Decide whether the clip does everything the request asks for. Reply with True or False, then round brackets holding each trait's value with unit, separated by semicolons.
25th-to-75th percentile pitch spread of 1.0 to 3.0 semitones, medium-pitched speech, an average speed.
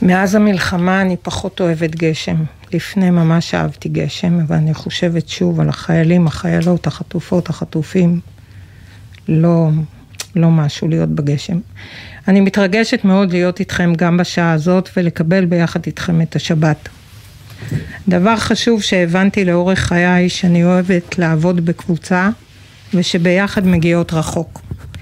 True (2.7 semitones; 170 Hz; 120 wpm)